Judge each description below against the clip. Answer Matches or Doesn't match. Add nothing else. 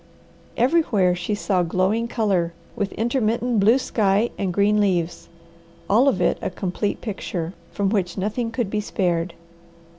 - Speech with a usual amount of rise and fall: Matches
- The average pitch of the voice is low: Doesn't match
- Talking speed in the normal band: Matches